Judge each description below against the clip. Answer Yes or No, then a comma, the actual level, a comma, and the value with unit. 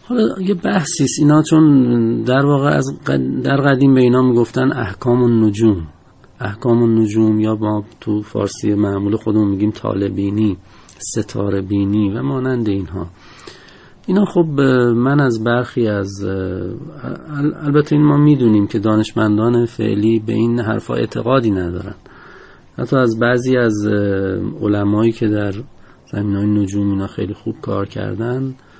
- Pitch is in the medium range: No, low, 115 Hz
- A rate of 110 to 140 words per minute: Yes, average, 135 wpm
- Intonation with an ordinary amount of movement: Yes, average, 4.1 semitones